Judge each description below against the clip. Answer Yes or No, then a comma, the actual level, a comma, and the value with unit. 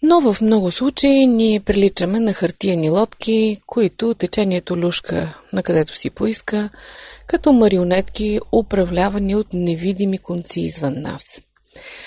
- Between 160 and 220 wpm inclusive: No, average, 120 wpm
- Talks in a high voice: Yes, high, 205 Hz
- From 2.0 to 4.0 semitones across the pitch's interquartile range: Yes, average, 3.7 semitones